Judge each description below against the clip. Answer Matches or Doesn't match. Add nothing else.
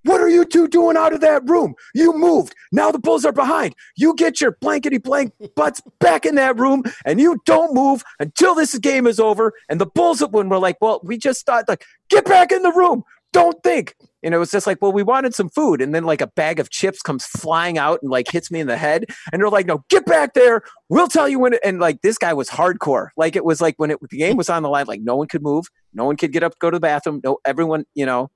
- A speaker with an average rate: Doesn't match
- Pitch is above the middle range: Matches